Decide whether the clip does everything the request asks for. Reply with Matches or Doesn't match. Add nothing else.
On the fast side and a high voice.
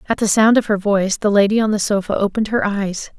Matches